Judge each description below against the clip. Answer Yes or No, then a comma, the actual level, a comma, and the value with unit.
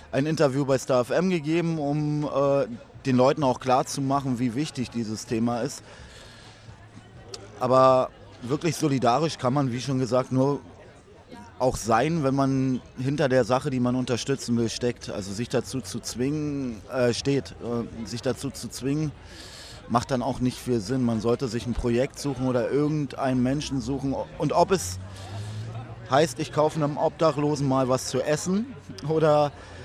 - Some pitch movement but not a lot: Yes, average, 3.1 semitones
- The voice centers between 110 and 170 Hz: Yes, low, 130 Hz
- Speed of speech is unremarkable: Yes, average, 165 wpm